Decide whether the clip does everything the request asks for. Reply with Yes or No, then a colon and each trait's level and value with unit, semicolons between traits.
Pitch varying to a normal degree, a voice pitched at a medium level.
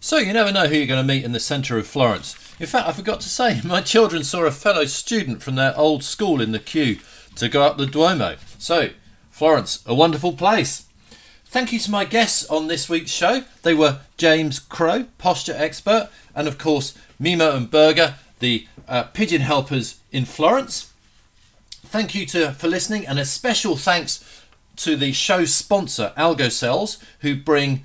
Yes: average, 4.5 semitones; medium, 150 Hz